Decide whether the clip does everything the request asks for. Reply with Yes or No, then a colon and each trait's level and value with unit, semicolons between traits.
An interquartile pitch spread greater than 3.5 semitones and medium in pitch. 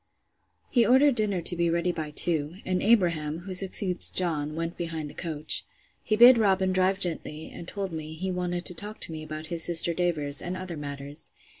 No: average, 3.0 semitones; medium, 175 Hz